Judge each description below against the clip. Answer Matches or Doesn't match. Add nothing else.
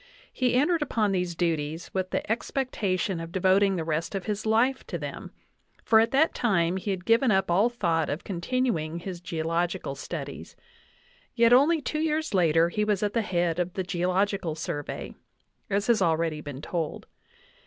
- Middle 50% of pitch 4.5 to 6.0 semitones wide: Matches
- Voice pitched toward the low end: Doesn't match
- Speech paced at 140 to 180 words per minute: Matches